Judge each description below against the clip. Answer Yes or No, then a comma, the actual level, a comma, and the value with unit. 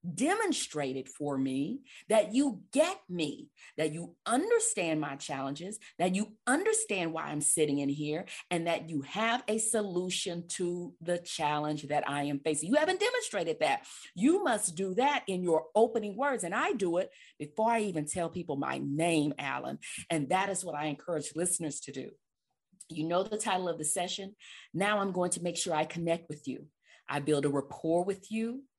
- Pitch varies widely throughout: Yes, wide, 5.7 semitones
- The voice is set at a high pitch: No, medium, 175 Hz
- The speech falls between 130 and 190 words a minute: Yes, average, 185 wpm